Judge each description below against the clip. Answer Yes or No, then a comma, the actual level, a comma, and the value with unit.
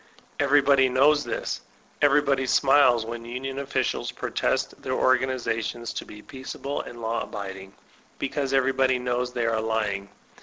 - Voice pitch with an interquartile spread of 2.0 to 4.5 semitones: Yes, average, 2.9 semitones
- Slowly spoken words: Yes, slow, 130 wpm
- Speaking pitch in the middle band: No, low, 130 Hz